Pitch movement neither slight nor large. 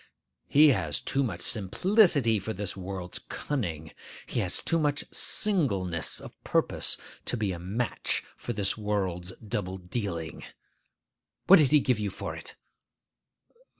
No: wide, 6.5 semitones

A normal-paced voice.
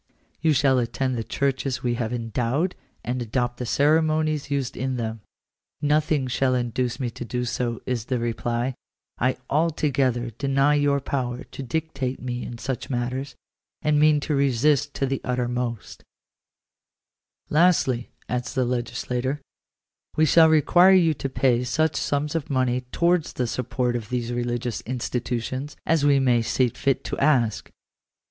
Yes: average, 155 wpm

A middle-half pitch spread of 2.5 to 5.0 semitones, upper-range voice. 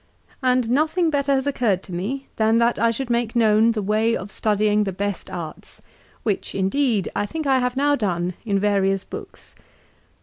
Yes: average, 4.4 semitones; high, 225 Hz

